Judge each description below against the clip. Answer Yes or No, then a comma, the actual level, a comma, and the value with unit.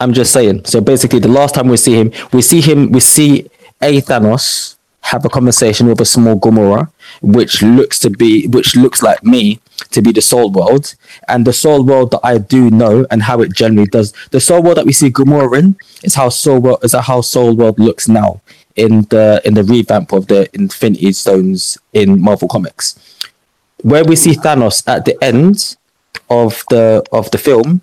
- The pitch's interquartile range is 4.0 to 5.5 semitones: Yes, average, 4.4 semitones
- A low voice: Yes, low, 125 Hz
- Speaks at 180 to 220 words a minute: Yes, average, 200 wpm